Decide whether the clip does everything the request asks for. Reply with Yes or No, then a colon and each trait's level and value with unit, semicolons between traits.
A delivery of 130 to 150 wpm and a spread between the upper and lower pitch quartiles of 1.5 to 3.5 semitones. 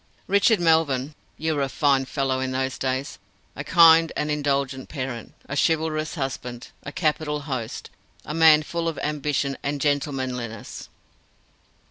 Yes: average, 140 wpm; average, 2.9 semitones